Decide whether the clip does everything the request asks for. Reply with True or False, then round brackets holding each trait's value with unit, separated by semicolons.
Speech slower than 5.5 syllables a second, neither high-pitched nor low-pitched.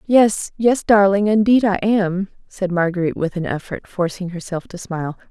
False (5.0 syllables/s; 195 Hz)